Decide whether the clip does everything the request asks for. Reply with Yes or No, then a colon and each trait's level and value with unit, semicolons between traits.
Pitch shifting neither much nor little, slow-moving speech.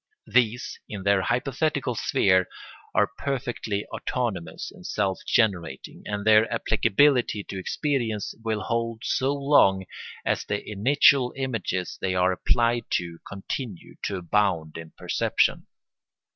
Yes: average, 4.6 semitones; slow, 120 wpm